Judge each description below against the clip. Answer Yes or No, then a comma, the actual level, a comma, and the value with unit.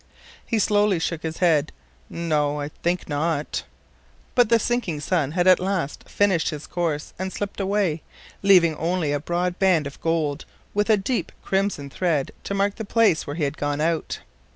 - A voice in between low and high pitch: Yes, medium, 170 Hz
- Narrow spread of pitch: No, average, 4.5 semitones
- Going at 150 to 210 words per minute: Yes, average, 175 wpm